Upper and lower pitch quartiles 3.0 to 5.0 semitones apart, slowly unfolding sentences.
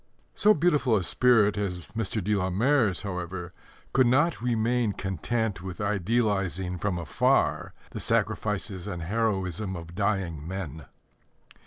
Yes: average, 4.0 semitones; slow, 130 wpm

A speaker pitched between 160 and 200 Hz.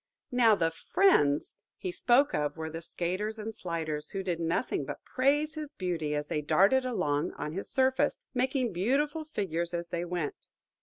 Yes: medium, 185 Hz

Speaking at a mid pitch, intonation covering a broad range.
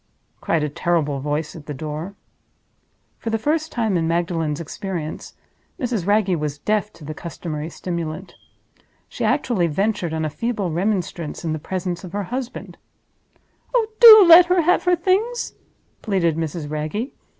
Yes: medium, 175 Hz; wide, 6.2 semitones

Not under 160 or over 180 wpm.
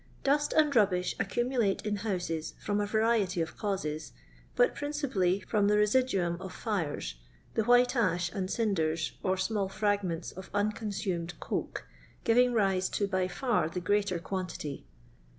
No: average, 150 wpm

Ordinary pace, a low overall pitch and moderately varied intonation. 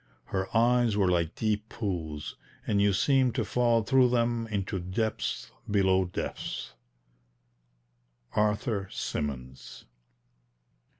No: slow, 105 wpm; low, 105 Hz; average, 4.0 semitones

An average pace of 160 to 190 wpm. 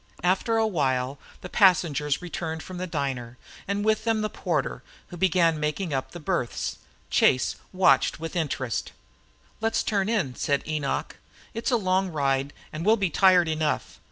Yes: average, 165 wpm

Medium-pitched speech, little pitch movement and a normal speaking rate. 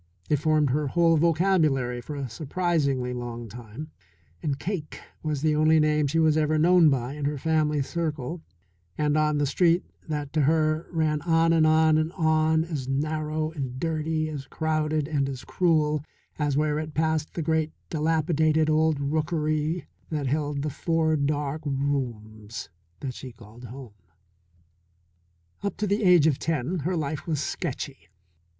Yes: medium, 155 Hz; narrow, 2.2 semitones; average, 160 wpm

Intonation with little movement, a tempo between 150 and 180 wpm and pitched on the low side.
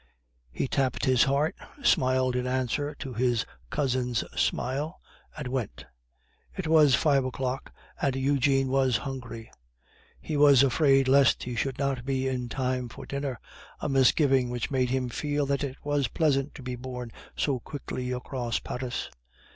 Yes: narrow, 1.8 semitones; average, 155 wpm; low, 130 Hz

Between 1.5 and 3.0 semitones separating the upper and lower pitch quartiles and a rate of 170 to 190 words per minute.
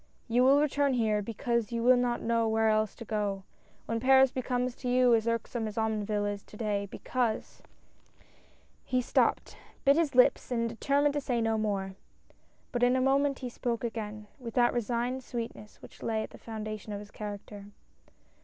Yes: average, 2.7 semitones; average, 185 wpm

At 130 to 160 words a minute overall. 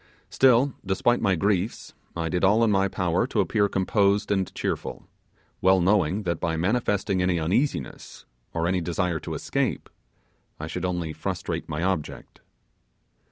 Yes: average, 150 wpm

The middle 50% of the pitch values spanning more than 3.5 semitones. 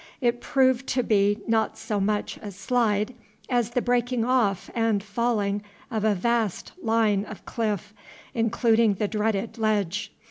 No: narrow, 2.5 semitones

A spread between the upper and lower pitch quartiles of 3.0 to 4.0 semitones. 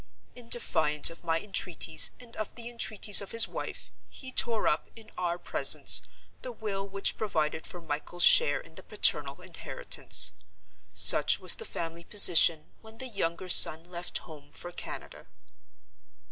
No: average, 5.3 semitones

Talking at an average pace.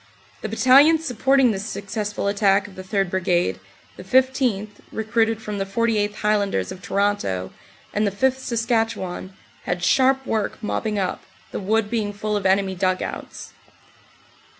Yes: average, 150 wpm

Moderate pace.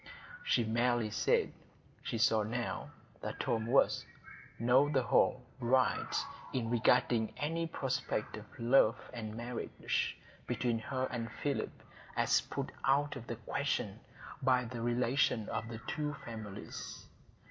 No: slow, 130 wpm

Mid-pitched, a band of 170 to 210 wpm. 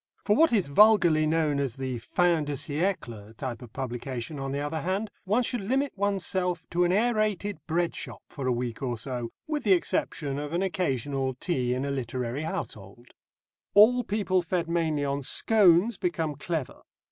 Yes: medium, 160 Hz; average, 175 wpm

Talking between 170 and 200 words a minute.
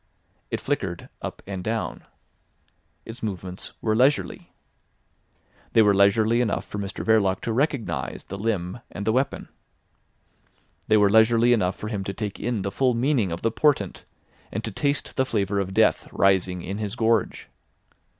No: average, 160 wpm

